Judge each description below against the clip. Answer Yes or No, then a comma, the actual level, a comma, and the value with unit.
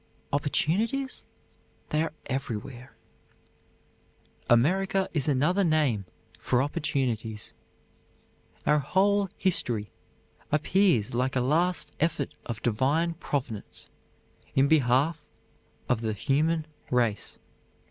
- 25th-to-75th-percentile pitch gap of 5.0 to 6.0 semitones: Yes, average, 5.3 semitones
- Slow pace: Yes, slow, 90 wpm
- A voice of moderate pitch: Yes, medium, 145 Hz